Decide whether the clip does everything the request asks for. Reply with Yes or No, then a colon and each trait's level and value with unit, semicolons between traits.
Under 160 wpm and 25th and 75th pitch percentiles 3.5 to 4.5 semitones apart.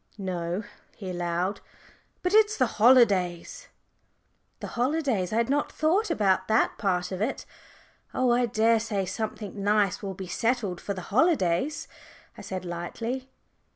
No: average, 140 wpm; average, 5.2 semitones